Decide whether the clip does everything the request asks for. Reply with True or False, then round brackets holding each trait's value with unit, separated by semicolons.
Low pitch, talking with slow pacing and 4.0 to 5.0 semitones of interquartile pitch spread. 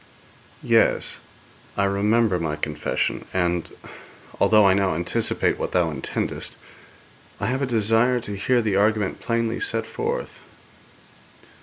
True (105 Hz; 125 wpm; 4.3 semitones)